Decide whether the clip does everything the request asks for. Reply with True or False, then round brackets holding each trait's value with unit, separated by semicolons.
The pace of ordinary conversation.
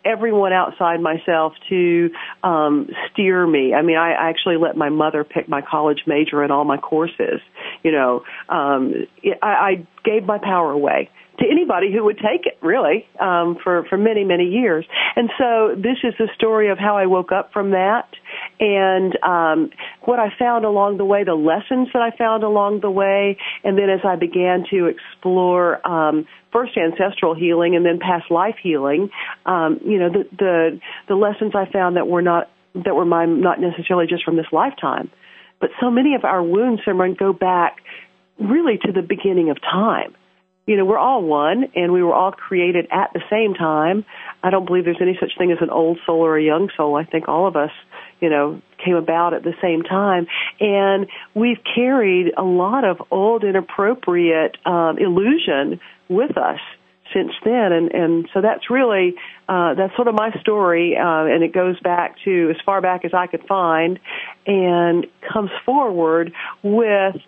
True (185 wpm)